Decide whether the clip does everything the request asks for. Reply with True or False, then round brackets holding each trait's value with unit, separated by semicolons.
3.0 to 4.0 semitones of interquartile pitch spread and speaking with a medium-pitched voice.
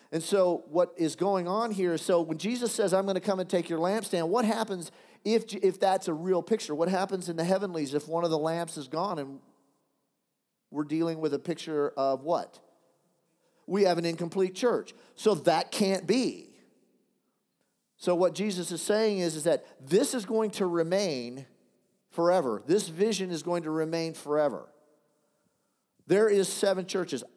True (3.3 semitones; 180 Hz)